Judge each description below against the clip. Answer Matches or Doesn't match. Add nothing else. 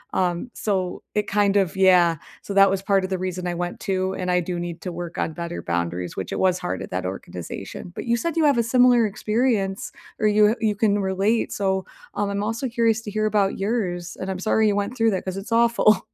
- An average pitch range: Matches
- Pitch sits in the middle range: Doesn't match